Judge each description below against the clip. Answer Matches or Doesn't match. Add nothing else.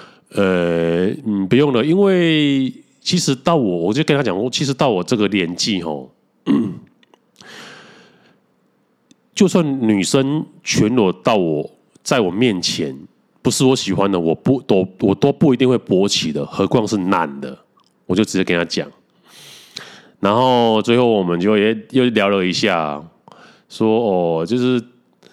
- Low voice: Matches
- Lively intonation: Matches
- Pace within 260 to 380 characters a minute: Doesn't match